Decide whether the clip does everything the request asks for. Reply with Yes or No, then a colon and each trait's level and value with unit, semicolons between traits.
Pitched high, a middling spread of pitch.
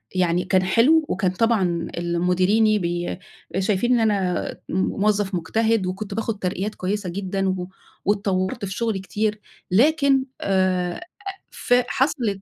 Yes: high, 195 Hz; average, 3.1 semitones